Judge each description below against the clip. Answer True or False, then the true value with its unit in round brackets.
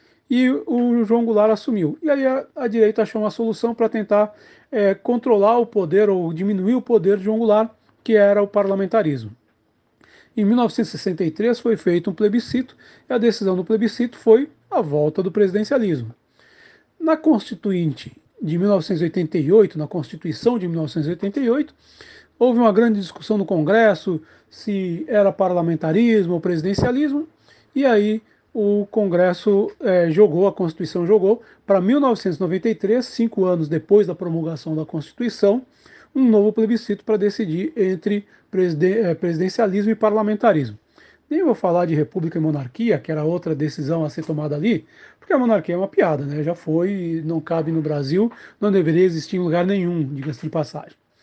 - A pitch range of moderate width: True (4.7 semitones)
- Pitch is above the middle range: True (200 Hz)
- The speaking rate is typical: True (150 wpm)